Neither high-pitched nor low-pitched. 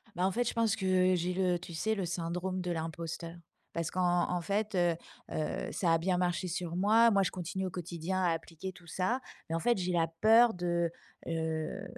Yes: medium, 180 Hz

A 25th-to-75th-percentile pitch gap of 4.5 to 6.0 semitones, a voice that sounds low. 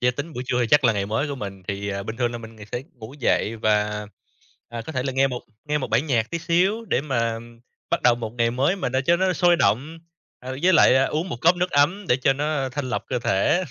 Yes: average, 5.1 semitones; low, 130 Hz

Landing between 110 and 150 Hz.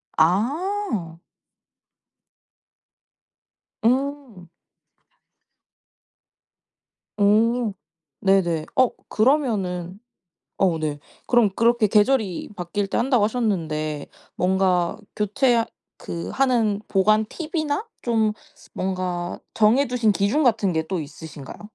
No: high, 210 Hz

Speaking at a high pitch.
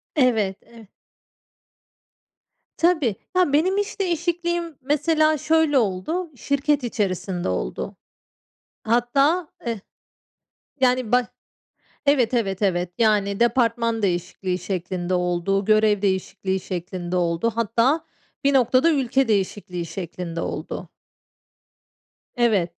Yes: high, 230 Hz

